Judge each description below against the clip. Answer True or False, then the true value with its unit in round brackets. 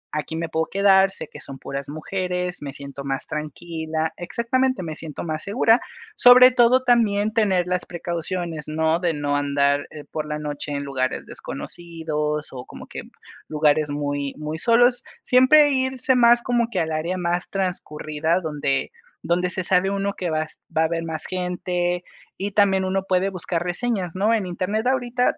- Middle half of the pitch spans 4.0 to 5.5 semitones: True (4.7 semitones)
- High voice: False (175 Hz)